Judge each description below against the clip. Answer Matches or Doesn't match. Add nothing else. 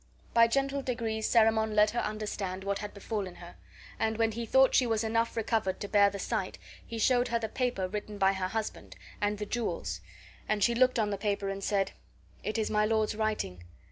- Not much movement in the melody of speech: Matches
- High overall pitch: Matches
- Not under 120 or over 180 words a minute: Doesn't match